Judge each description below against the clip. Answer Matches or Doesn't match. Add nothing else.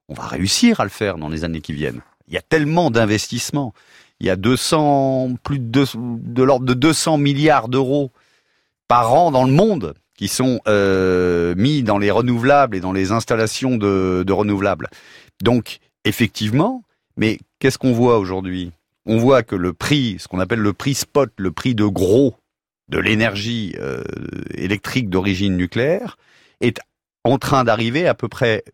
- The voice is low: Matches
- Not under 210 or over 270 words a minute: Doesn't match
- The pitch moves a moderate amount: Doesn't match